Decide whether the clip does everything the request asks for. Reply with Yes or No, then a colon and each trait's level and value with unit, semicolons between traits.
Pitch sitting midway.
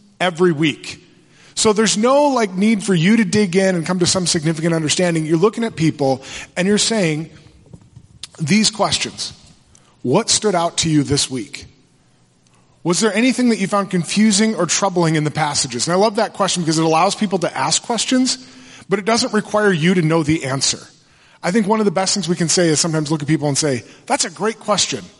Yes: medium, 180 Hz